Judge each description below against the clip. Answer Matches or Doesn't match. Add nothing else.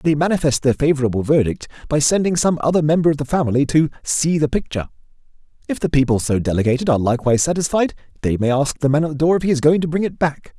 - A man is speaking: Matches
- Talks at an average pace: Doesn't match